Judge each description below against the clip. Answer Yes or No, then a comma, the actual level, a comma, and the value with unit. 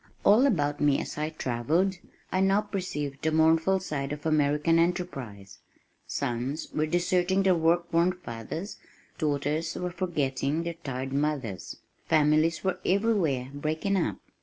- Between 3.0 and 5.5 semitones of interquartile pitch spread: Yes, average, 3.9 semitones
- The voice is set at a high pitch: No, medium, 160 Hz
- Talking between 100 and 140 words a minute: Yes, slow, 135 wpm